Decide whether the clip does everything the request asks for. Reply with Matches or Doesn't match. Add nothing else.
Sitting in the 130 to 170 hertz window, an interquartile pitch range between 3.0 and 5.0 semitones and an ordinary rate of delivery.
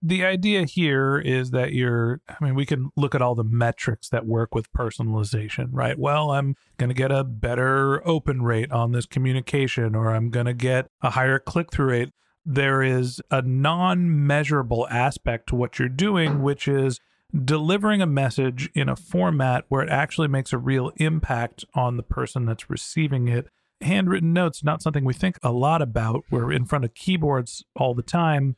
Matches